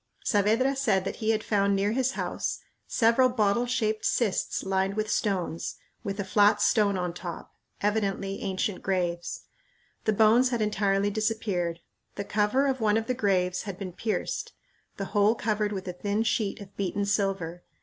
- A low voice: No, high, 205 Hz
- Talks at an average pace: Yes, average, 170 wpm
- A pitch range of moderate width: No, narrow, 2.2 semitones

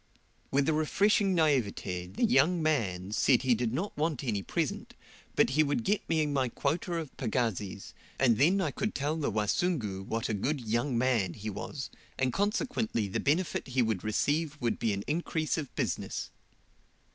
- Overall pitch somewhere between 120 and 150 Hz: Yes, low, 135 Hz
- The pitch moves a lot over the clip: Yes, wide, 6.4 semitones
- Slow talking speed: No, average, 170 wpm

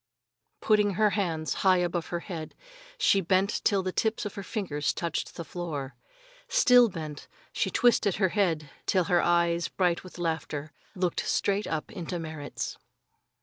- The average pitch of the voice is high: No, medium, 175 Hz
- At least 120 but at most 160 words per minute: Yes, average, 150 wpm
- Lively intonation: No, average, 3.5 semitones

